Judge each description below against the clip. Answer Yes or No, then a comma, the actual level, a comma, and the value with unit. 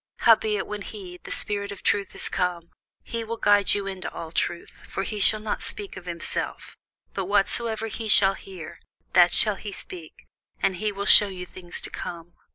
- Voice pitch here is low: No, high, 195 Hz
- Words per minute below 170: No, average, 190 wpm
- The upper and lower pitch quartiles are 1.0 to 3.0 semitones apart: Yes, narrow, 2.6 semitones